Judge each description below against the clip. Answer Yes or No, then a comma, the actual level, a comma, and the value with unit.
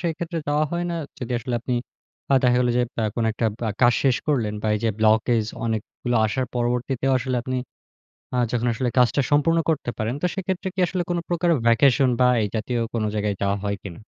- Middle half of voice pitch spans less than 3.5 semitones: No, average, 4.5 semitones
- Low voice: Yes, low, 125 Hz